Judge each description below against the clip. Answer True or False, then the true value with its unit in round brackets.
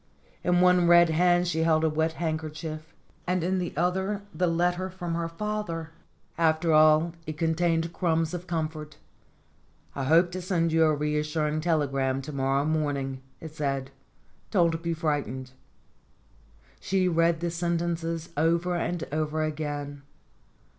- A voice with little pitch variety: True (2.0 semitones)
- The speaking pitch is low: False (165 Hz)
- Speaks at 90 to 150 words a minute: True (145 wpm)